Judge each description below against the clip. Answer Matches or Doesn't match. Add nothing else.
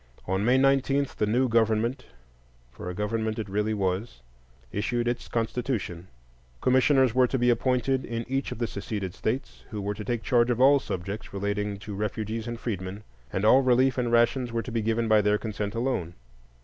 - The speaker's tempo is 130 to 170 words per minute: Doesn't match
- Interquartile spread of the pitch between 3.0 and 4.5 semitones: Matches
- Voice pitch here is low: Matches